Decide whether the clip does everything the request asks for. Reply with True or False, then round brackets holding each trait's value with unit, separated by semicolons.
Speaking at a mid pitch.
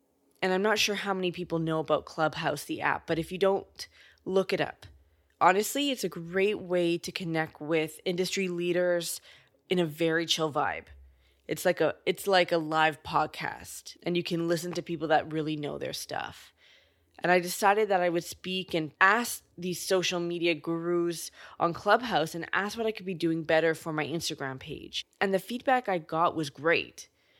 True (170 Hz)